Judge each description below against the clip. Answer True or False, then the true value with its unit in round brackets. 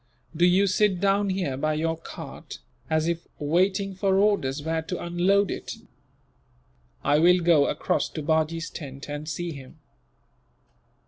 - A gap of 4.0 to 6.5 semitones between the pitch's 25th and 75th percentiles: False (3.6 semitones)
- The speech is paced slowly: False (145 wpm)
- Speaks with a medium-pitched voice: True (170 Hz)